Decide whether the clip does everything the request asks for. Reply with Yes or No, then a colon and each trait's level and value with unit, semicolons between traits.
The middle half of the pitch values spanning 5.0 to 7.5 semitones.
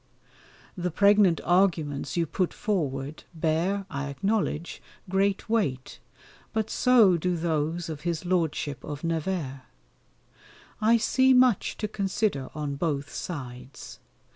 Yes: average, 5.3 semitones